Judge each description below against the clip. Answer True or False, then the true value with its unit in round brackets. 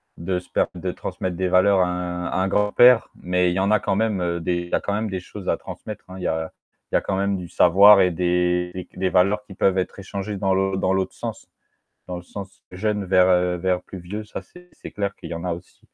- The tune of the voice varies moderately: False (1.8 semitones)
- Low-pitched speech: True (95 Hz)